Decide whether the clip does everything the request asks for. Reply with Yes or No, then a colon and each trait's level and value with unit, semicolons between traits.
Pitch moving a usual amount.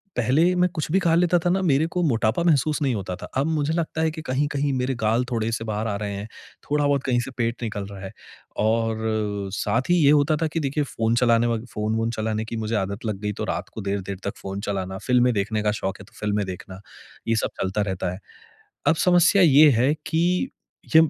No: wide, 5.9 semitones